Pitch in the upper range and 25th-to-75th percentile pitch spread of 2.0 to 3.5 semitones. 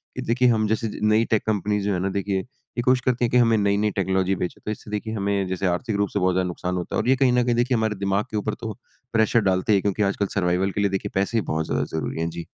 No: low, 100 Hz; average, 2.8 semitones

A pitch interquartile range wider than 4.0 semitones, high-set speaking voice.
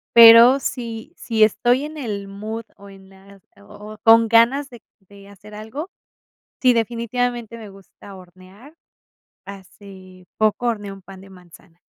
No: average, 3.1 semitones; high, 215 Hz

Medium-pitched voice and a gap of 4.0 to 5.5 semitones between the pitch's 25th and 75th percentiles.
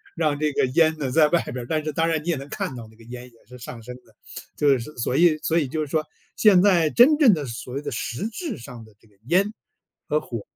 Yes: medium, 150 Hz; average, 5.1 semitones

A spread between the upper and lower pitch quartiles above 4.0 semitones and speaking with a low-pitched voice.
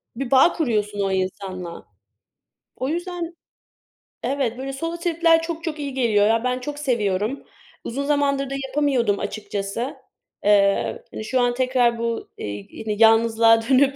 No: average, 5.0 semitones; very high, 250 Hz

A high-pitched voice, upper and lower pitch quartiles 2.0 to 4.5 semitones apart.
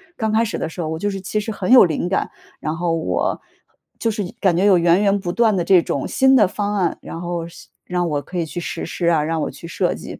No: medium, 180 Hz; average, 3.5 semitones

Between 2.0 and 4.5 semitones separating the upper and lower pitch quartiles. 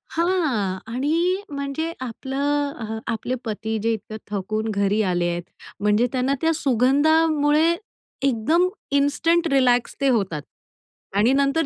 No: average, 5.2 semitones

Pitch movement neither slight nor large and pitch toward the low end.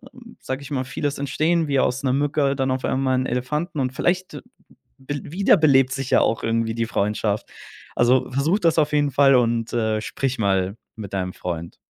Yes: average, 4.0 semitones; low, 130 Hz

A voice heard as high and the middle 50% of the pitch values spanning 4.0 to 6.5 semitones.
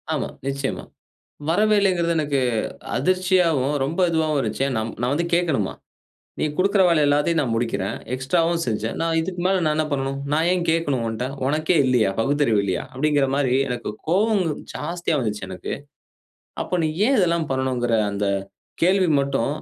No: medium, 150 Hz; average, 4.9 semitones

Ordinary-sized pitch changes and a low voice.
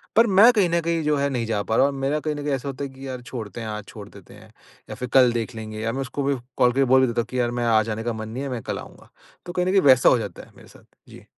Yes: average, 3.9 semitones; low, 130 Hz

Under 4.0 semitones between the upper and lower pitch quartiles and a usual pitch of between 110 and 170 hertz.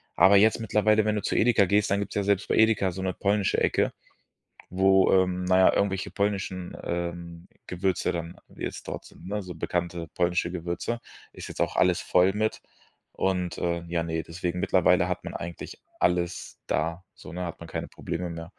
No: narrow, 2.5 semitones; very low, 90 Hz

